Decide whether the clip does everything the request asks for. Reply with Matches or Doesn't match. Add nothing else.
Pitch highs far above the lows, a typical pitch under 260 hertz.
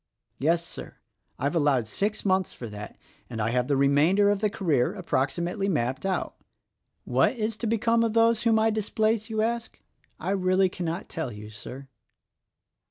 Matches